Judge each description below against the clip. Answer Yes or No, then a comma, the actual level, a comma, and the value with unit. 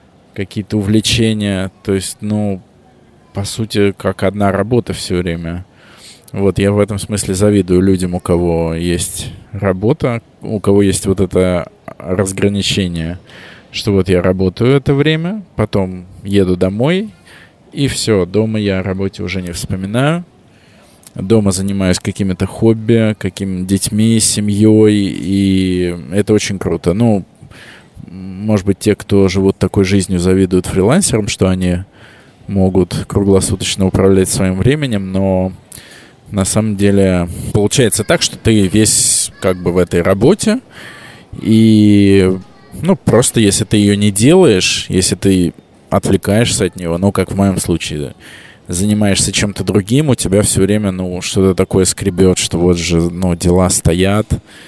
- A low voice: Yes, low, 100 Hz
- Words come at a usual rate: Yes, average, 135 wpm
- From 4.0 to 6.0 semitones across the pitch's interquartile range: No, narrow, 2.4 semitones